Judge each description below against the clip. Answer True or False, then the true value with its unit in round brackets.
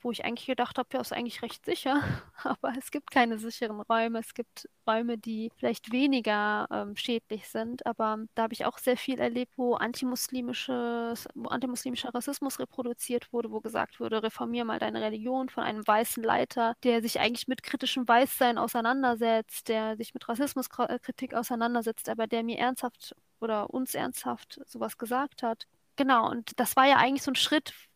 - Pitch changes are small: True (2.1 semitones)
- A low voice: False (240 Hz)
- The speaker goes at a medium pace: True (180 wpm)